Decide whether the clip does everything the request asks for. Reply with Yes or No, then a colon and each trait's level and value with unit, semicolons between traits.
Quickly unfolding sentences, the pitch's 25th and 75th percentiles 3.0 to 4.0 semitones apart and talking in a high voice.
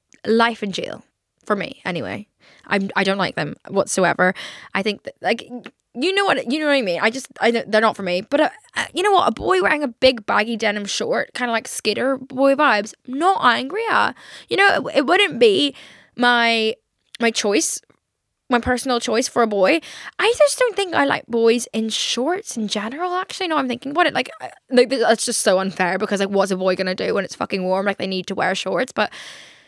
No: fast, 220 wpm; wide, 5.6 semitones; high, 240 Hz